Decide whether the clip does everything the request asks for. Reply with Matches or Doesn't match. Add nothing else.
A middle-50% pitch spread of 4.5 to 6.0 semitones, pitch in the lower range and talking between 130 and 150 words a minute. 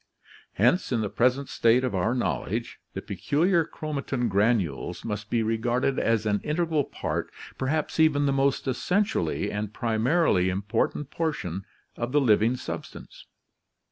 Matches